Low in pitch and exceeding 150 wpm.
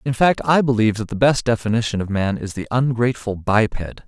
Yes: low, 115 Hz; fast, 205 wpm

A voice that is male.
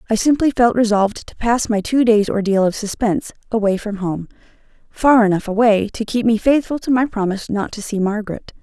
No: female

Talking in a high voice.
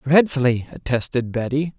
No: low, 135 Hz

